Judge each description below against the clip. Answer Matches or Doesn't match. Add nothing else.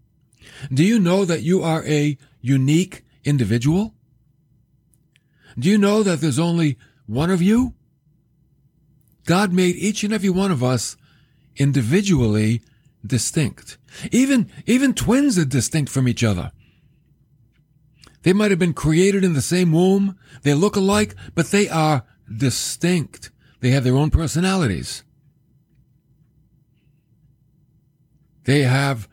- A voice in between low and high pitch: Matches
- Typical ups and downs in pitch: Matches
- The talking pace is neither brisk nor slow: Doesn't match